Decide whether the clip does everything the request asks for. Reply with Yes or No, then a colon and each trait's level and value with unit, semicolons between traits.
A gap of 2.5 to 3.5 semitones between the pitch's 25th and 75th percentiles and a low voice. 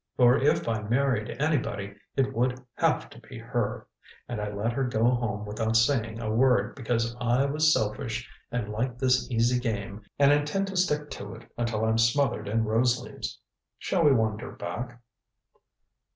Yes: average, 3.1 semitones; low, 120 Hz